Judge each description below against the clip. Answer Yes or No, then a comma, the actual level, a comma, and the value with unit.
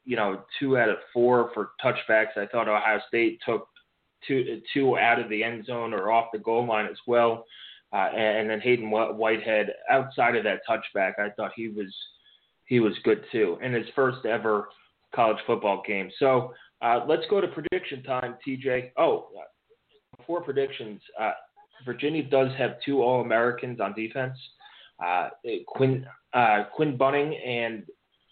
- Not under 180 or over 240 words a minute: No, average, 165 wpm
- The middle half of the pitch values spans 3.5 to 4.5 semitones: Yes, average, 4.0 semitones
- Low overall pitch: Yes, low, 120 Hz